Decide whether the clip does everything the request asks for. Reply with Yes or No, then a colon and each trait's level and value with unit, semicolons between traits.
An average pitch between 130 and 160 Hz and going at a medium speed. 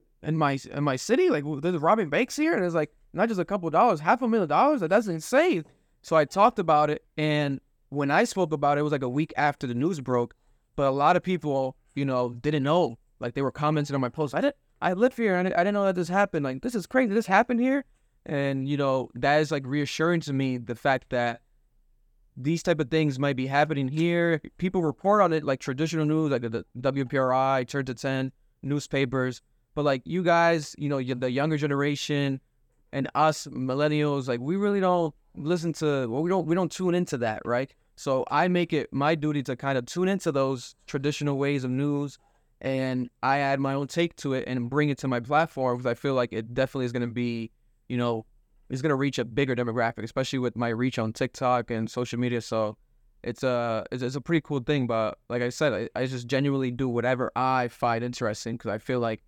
No: medium, 140 Hz; fast, 230 wpm